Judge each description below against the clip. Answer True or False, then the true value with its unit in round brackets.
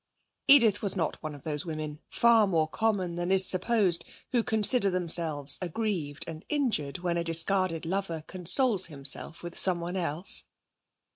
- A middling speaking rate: True (150 wpm)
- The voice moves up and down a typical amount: True (3.9 semitones)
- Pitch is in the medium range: True (175 Hz)